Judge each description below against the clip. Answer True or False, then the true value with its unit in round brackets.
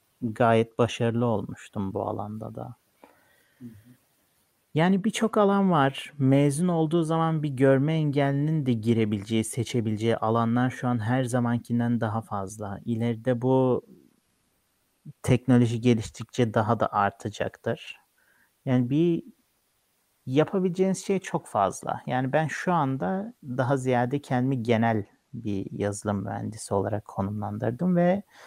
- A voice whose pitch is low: True (125 Hz)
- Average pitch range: True (4.3 semitones)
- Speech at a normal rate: True (110 wpm)